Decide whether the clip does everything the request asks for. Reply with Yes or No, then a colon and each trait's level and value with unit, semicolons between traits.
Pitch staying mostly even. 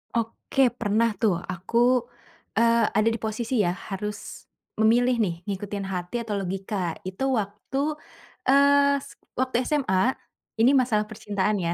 No: average, 3.6 semitones